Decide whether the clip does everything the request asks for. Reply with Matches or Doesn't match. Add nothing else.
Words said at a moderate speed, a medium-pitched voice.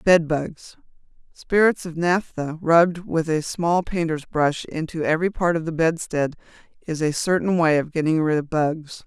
Matches